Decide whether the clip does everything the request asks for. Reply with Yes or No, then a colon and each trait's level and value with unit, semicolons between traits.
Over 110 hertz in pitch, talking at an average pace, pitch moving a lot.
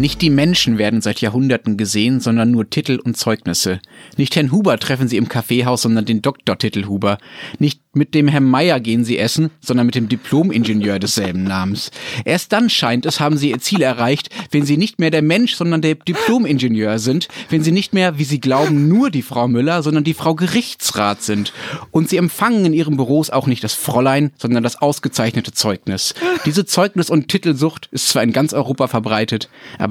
No: low, 135 Hz; fast, 195 wpm; wide, 5.9 semitones